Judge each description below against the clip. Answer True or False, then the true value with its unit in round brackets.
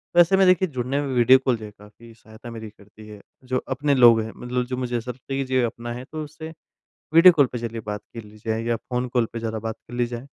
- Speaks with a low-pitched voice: True (120 Hz)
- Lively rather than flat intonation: False (2.8 semitones)